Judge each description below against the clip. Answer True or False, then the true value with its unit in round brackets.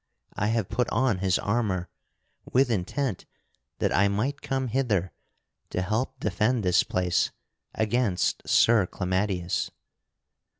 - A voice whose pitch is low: True (105 Hz)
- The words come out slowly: True (120 wpm)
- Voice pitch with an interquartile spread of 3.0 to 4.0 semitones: False (4.7 semitones)